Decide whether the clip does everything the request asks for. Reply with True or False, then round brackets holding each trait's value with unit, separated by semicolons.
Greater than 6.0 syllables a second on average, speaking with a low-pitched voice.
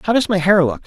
False (7.3 syllables/s; 185 Hz)